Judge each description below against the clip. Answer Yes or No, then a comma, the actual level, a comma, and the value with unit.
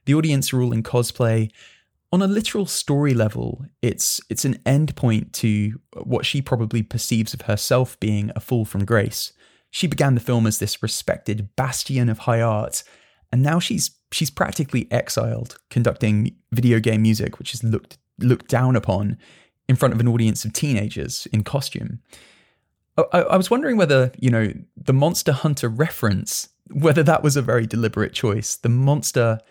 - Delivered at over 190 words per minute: No, average, 170 wpm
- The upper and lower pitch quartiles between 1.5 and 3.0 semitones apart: No, average, 3.8 semitones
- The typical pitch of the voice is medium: No, low, 120 Hz